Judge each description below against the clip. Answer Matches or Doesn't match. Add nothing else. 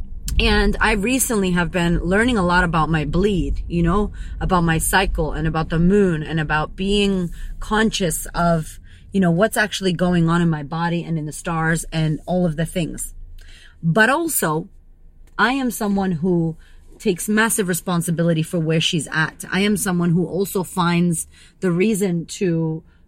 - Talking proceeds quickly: Doesn't match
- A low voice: Doesn't match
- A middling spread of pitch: Matches